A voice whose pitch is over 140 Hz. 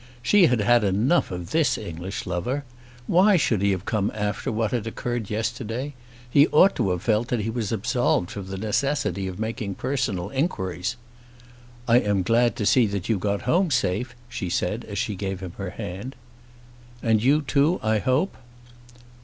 No: low, 110 Hz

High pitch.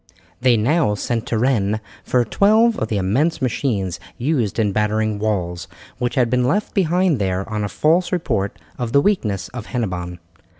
No: low, 115 Hz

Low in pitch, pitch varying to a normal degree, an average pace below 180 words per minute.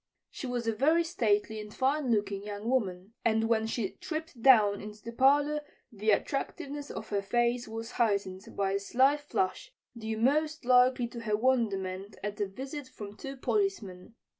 No: high, 230 Hz; average, 4.4 semitones; average, 170 wpm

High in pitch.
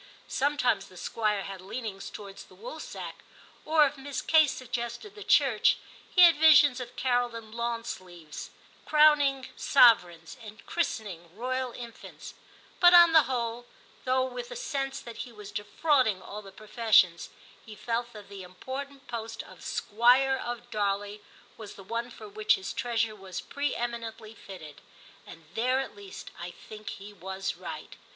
Yes: high, 235 Hz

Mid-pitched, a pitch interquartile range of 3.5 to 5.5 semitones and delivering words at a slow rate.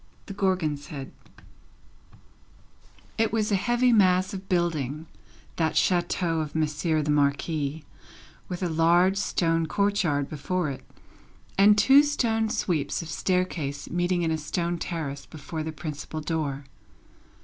Yes: medium, 165 Hz; average, 3.8 semitones; slow, 130 wpm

